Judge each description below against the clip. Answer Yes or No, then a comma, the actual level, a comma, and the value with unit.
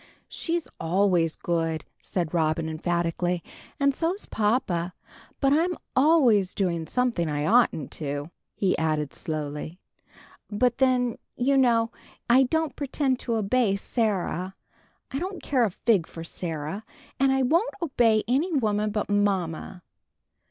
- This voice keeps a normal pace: No, slow, 130 wpm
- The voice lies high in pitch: Yes, high, 210 Hz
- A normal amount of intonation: No, wide, 7.4 semitones